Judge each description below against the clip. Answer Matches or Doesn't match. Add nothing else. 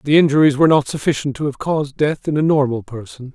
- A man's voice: Matches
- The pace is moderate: Doesn't match